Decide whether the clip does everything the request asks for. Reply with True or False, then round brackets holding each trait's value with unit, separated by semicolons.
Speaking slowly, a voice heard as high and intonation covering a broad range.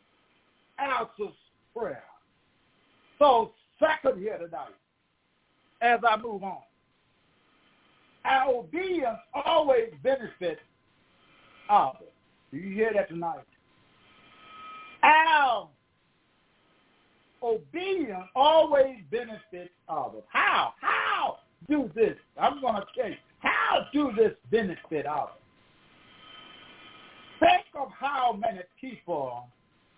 True (85 wpm; 275 Hz; 8.4 semitones)